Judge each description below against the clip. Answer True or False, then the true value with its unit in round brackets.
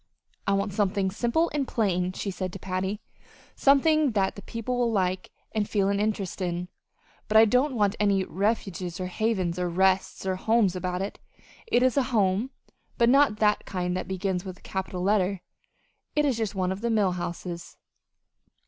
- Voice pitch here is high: True (195 Hz)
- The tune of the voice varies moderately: True (3.3 semitones)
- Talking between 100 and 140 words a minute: False (185 wpm)